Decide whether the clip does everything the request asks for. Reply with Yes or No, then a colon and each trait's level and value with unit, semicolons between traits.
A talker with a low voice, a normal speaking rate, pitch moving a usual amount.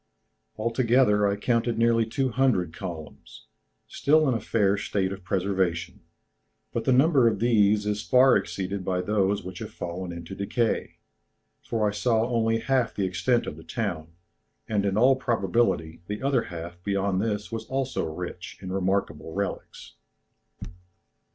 Yes: low, 105 Hz; average, 150 wpm; average, 4.0 semitones